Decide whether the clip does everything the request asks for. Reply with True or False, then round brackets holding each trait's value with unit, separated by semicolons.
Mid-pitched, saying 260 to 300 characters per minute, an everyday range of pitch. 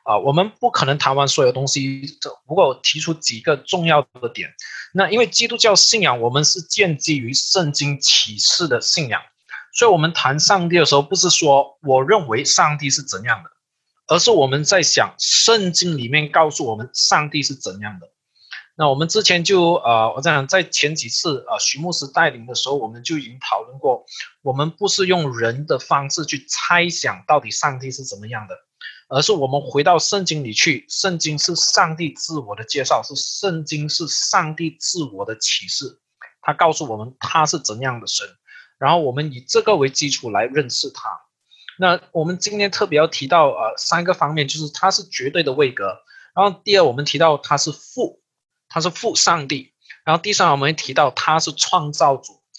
True (155 Hz; 285 characters per minute; 4.3 semitones)